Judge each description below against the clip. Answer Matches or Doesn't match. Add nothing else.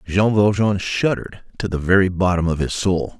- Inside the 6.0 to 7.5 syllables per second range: Doesn't match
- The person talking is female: Doesn't match